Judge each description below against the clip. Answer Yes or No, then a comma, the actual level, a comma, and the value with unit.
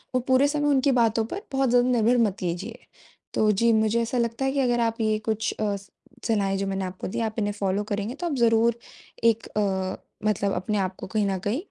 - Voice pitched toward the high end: Yes, high, 225 Hz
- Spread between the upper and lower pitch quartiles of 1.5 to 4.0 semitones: Yes, average, 3.2 semitones